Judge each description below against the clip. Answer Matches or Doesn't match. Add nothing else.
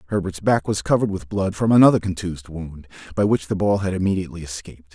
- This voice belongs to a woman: Doesn't match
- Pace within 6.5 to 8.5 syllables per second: Matches